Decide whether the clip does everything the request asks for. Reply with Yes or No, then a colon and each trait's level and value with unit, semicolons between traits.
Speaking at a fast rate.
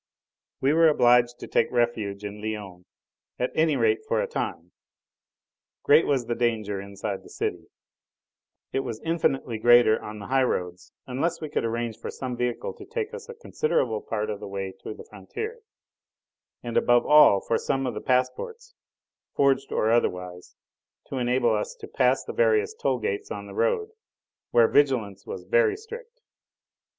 No: average, 170 wpm